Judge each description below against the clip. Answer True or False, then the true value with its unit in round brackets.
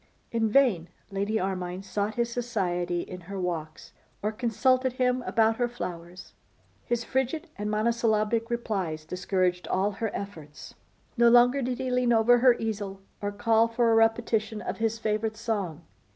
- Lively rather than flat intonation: False (3.8 semitones)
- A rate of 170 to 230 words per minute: False (155 wpm)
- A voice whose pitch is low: False (220 Hz)